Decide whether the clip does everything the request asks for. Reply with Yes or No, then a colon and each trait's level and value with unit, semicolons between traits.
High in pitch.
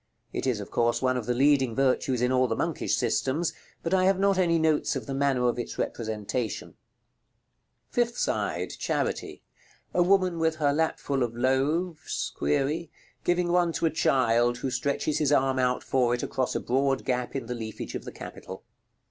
No: low, 135 Hz